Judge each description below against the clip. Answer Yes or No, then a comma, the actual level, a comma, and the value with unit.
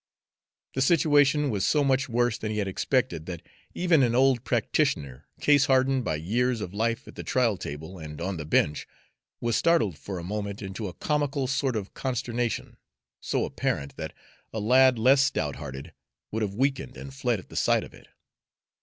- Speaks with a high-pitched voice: No, low, 120 Hz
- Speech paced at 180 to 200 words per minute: Yes, average, 185 wpm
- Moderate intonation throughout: No, wide, 5.8 semitones